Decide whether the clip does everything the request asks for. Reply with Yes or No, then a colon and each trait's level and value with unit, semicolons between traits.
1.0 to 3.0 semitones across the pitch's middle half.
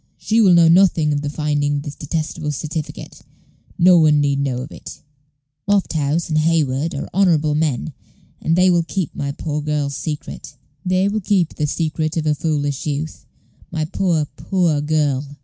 Yes: narrow, 2.6 semitones